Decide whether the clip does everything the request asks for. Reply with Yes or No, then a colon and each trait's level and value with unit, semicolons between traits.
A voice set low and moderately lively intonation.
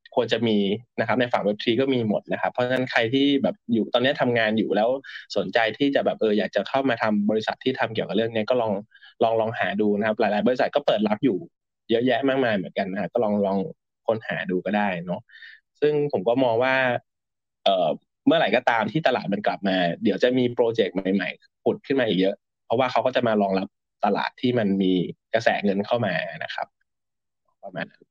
Yes: low, 110 Hz; average, 4.0 semitones